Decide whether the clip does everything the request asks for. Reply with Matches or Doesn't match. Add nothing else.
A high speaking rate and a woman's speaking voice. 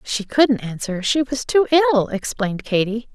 Doesn't match